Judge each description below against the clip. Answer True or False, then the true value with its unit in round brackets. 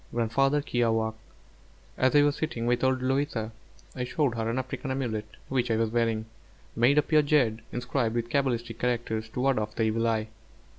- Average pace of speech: True (185 wpm)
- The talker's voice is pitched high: False (120 Hz)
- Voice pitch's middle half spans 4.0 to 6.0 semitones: False (2.8 semitones)